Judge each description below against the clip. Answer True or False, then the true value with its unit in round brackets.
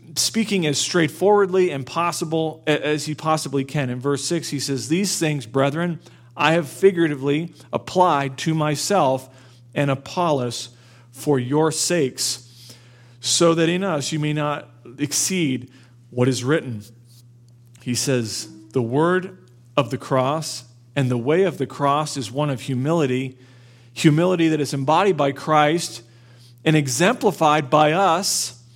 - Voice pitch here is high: False (140 Hz)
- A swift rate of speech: False (140 wpm)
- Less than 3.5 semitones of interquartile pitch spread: False (4.4 semitones)